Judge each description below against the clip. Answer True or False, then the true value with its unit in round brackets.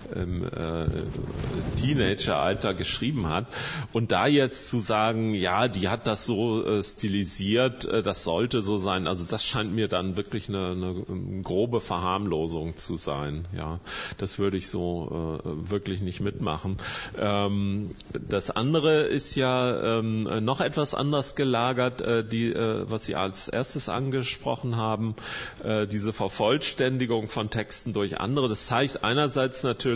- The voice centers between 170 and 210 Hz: False (110 Hz)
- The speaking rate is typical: True (145 wpm)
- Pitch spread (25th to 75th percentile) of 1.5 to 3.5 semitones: False (4.3 semitones)